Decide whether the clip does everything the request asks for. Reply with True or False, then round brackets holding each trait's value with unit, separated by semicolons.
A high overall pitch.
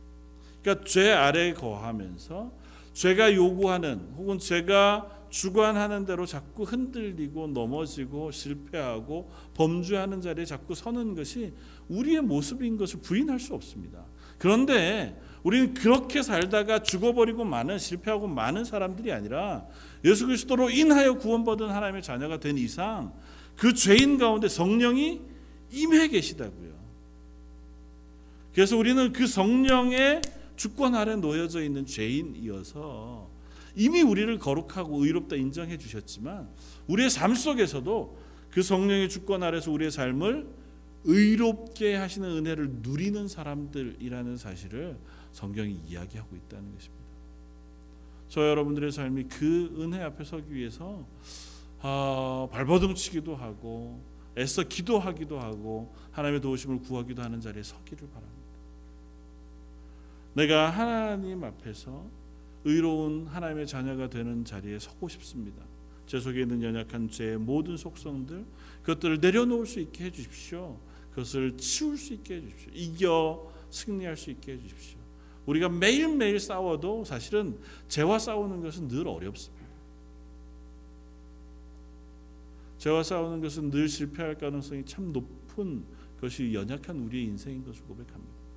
False (150 Hz)